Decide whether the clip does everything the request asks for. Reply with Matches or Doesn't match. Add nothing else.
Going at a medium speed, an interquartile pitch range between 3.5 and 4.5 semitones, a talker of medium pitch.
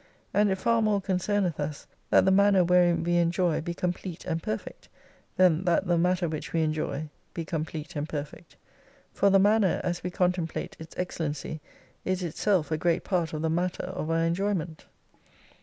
Doesn't match